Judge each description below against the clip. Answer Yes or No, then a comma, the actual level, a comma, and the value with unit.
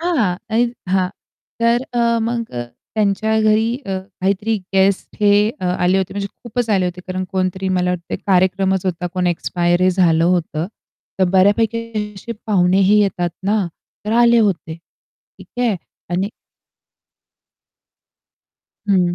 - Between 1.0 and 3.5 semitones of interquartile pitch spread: Yes, average, 3.2 semitones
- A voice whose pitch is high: Yes, high, 195 Hz